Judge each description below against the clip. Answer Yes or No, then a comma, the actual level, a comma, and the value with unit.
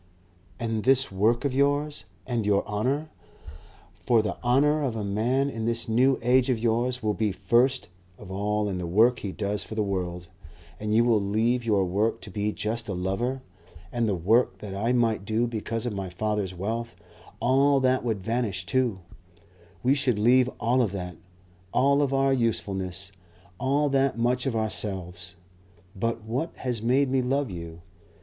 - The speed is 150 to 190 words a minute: Yes, average, 175 wpm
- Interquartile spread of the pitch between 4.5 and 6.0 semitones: No, average, 3.9 semitones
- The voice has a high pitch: No, low, 115 Hz